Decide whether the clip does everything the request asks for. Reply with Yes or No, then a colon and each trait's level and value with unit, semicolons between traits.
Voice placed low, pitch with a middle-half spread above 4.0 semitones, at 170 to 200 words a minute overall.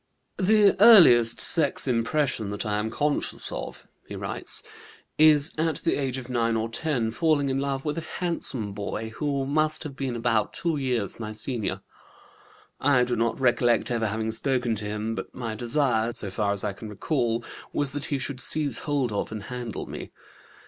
Yes: low, 125 Hz; average, 4.4 semitones; average, 185 wpm